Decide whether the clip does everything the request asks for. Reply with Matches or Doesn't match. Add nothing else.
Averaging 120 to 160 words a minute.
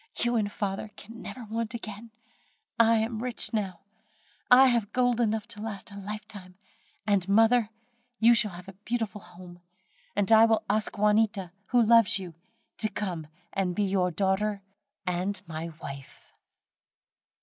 Matches